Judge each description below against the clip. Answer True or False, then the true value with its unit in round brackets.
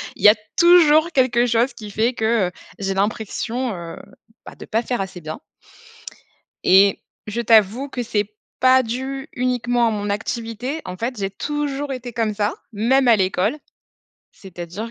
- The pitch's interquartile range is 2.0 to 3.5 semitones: False (3.9 semitones)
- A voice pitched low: False (230 Hz)